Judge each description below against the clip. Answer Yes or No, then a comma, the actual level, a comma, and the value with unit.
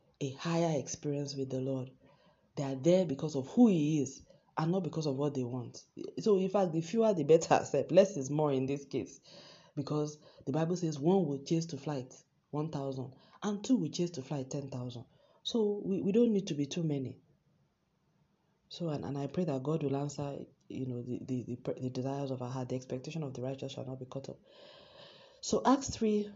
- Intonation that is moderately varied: Yes, average, 4.4 semitones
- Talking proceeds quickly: Yes, fast, 210 wpm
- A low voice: No, medium, 150 Hz